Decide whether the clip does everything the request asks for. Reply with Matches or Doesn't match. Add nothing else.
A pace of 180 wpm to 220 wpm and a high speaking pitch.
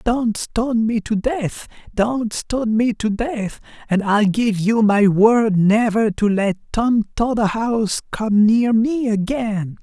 Doesn't match